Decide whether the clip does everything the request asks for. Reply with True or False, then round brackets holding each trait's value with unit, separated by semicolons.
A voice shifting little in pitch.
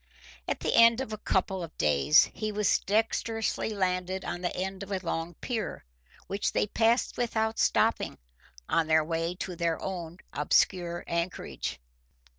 False (4.1 semitones)